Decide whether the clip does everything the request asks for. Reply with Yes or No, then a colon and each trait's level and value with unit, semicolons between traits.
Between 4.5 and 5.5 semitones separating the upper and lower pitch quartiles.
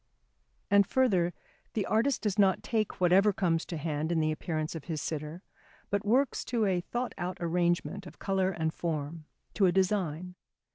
No: average, 3.7 semitones